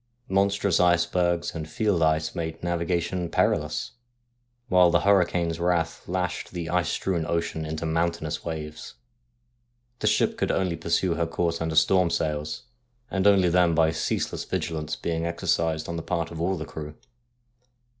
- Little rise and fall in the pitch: Yes, narrow, 1.7 semitones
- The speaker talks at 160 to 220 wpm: No, average, 150 wpm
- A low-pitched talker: Yes, very low, 85 Hz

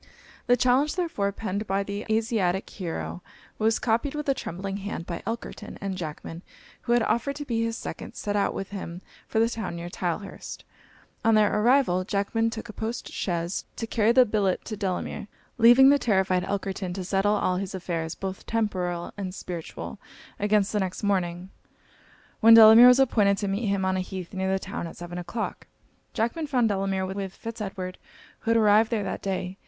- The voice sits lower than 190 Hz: No, high, 200 Hz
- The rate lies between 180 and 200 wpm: Yes, average, 190 wpm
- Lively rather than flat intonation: No, average, 3.3 semitones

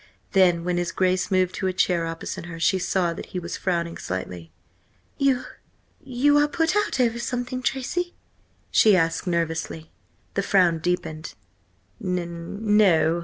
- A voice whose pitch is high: No, medium, 180 Hz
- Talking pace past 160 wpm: No, average, 145 wpm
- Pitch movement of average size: No, wide, 5.9 semitones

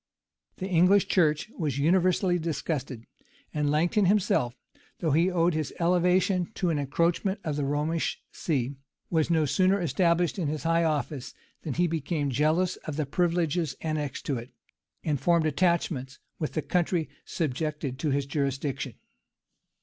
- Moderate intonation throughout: Yes, average, 3.4 semitones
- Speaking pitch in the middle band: Yes, medium, 160 Hz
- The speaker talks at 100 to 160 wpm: Yes, average, 150 wpm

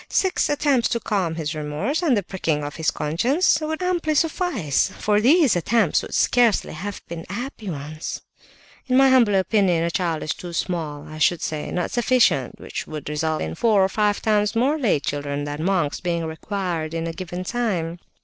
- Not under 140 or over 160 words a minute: No, average, 190 wpm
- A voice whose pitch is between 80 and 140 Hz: No, medium, 185 Hz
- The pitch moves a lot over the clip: Yes, wide, 7.1 semitones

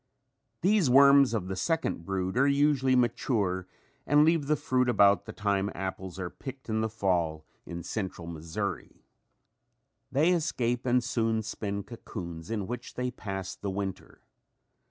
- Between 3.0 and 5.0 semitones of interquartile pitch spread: No, wide, 5.6 semitones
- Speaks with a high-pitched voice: No, low, 110 Hz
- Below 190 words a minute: Yes, average, 150 wpm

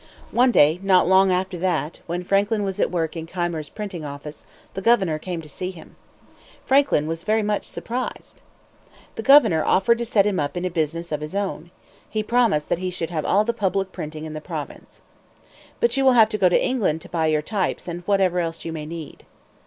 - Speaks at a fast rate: Yes, fast, 215 wpm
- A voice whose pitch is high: No, medium, 180 Hz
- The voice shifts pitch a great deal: No, average, 4.4 semitones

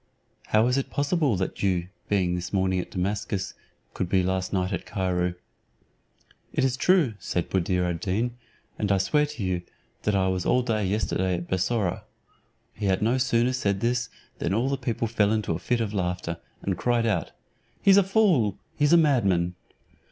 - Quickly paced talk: No, average, 185 wpm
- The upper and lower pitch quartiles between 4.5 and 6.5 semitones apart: Yes, average, 4.9 semitones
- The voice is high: No, low, 100 Hz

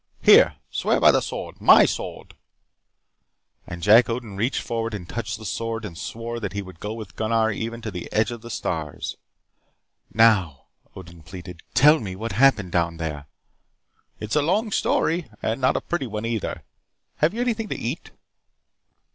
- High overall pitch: No, low, 110 Hz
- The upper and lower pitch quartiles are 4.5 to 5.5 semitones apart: No, average, 4.1 semitones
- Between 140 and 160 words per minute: No, average, 175 wpm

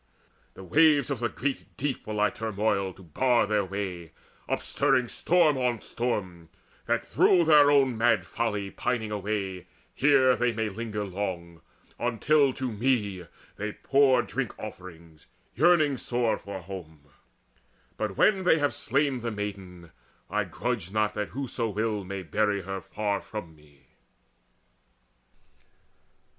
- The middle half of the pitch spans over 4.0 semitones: Yes, average, 5.0 semitones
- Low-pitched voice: Yes, low, 110 Hz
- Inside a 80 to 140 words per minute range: Yes, slow, 135 wpm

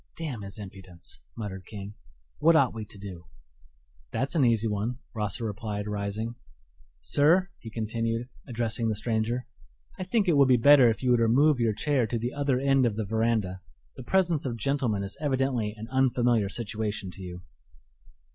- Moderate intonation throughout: Yes, average, 4.1 semitones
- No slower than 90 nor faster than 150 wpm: No, average, 175 wpm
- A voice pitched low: Yes, low, 115 Hz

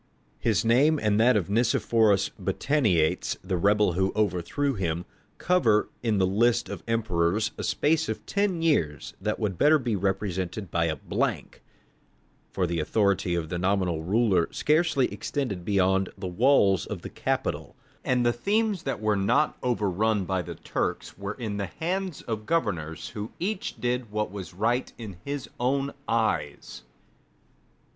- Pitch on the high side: No, low, 105 Hz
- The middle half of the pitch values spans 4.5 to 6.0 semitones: Yes, average, 5.0 semitones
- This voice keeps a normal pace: Yes, average, 155 wpm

